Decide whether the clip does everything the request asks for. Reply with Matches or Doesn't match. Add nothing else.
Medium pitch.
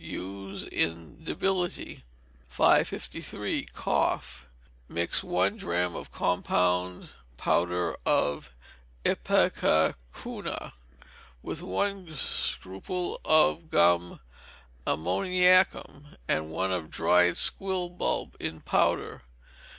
Doesn't match